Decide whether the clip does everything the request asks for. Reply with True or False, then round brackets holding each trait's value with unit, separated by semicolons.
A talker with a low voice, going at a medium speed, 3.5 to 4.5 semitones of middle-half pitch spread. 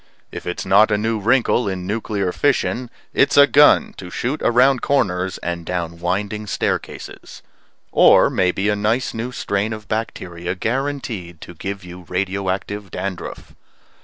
True (100 Hz; 150 wpm; 4.1 semitones)